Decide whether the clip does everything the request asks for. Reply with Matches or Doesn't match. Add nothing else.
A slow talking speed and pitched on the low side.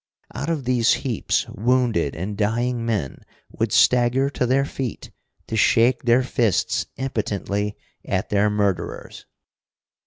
Matches